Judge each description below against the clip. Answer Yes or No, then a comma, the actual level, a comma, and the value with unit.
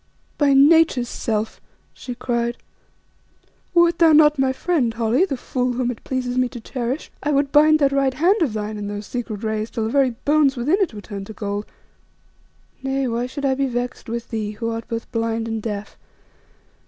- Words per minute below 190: No, average, 195 wpm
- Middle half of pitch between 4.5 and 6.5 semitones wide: No, average, 3.6 semitones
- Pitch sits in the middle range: No, high, 245 Hz